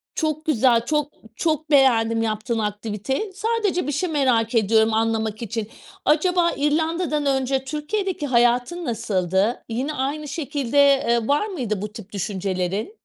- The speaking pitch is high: Yes, very high, 265 Hz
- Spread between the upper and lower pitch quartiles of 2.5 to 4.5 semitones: No, wide, 5.4 semitones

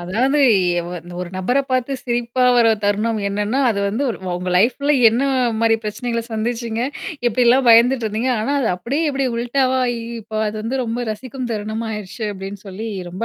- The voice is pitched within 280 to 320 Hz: No, high, 230 Hz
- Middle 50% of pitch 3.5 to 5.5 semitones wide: No, average, 3.0 semitones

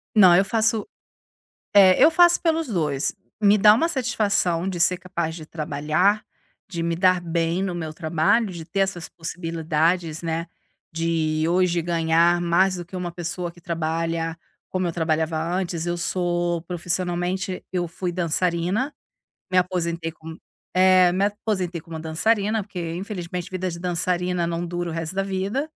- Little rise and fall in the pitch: Yes, narrow, 2.2 semitones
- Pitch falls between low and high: Yes, medium, 175 Hz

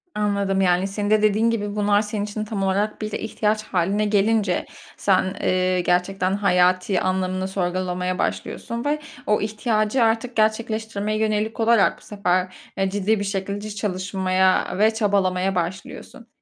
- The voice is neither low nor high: No, high, 200 Hz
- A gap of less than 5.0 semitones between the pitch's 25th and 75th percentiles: Yes, narrow, 2.4 semitones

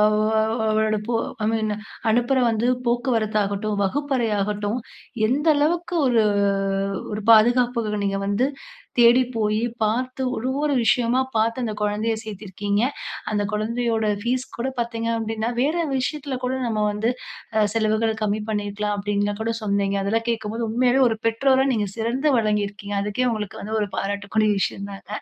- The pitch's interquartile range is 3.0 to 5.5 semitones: No, narrow, 2.5 semitones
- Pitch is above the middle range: Yes, high, 220 Hz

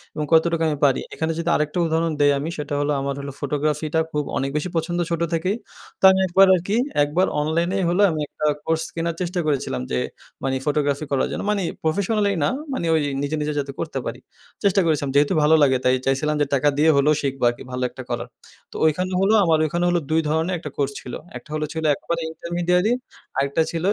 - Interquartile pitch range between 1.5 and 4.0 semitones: Yes, average, 3.0 semitones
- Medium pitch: Yes, medium, 155 Hz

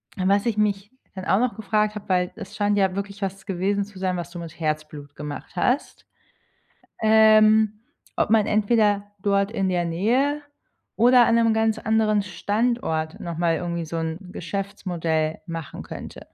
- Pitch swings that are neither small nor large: Yes, average, 3.8 semitones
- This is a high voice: Yes, high, 200 Hz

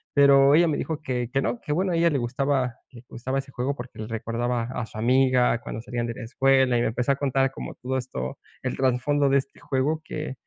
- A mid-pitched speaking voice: No, low, 130 Hz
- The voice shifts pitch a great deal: No, narrow, 2.4 semitones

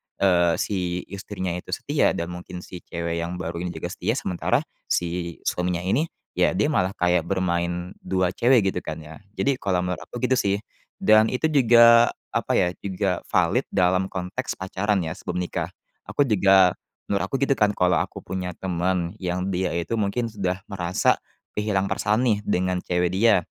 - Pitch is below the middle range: Yes, very low, 95 Hz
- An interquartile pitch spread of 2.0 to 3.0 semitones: Yes, average, 2.7 semitones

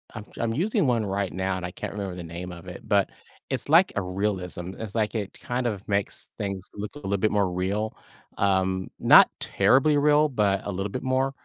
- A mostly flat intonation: No, average, 3.8 semitones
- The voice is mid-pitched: No, low, 100 Hz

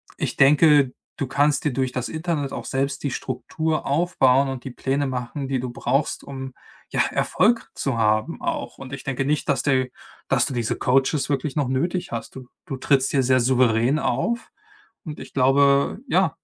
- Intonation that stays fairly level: Yes, narrow, 2.2 semitones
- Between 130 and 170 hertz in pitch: Yes, low, 135 Hz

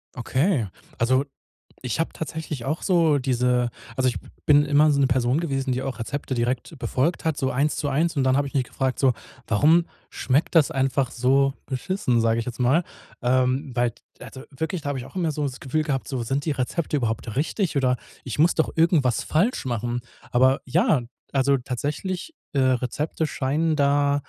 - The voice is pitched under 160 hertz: Yes, low, 135 Hz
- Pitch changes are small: No, average, 3.1 semitones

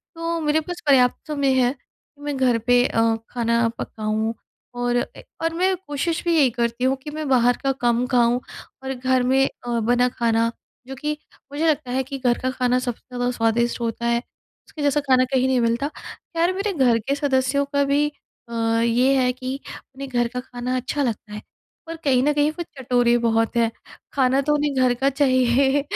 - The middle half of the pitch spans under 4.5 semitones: Yes, average, 2.9 semitones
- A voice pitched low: No, very high, 255 Hz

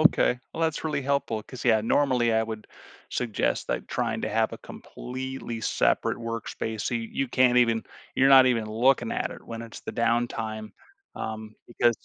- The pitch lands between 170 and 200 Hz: No, low, 120 Hz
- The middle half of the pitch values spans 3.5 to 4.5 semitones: No, narrow, 2.5 semitones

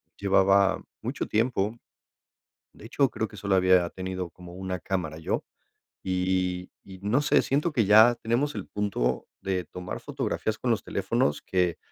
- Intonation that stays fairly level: No, average, 3.0 semitones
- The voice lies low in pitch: Yes, very low, 95 Hz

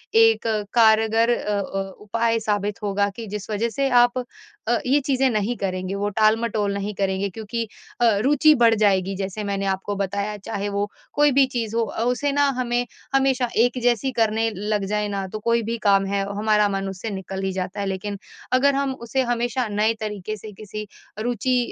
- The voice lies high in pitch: Yes, high, 215 Hz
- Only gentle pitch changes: No, average, 3.1 semitones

